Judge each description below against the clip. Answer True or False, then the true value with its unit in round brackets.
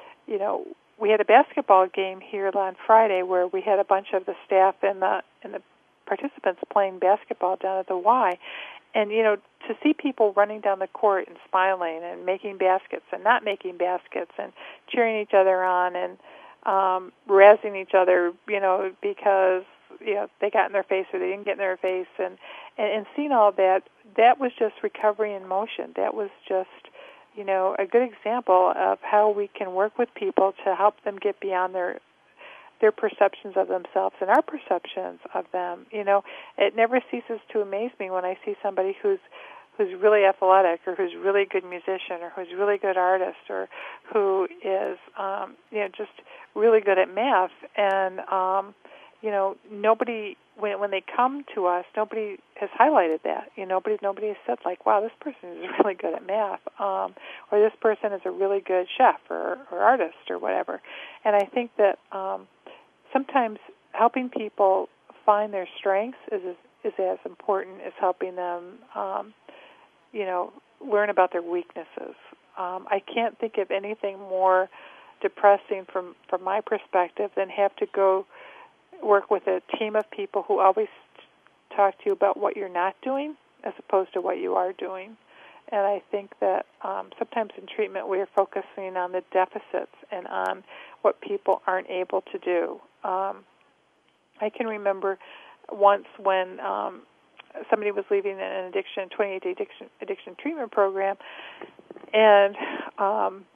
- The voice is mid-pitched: False (200 Hz)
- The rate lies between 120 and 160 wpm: False (175 wpm)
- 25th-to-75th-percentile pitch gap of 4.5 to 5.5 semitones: False (2.9 semitones)